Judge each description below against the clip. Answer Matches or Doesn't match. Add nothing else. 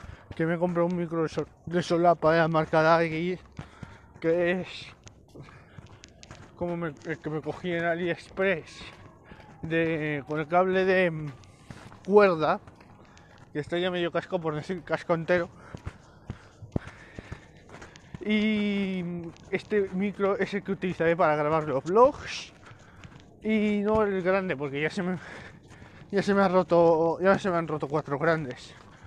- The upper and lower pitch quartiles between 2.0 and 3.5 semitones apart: Matches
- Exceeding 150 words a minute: Doesn't match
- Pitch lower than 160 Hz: Doesn't match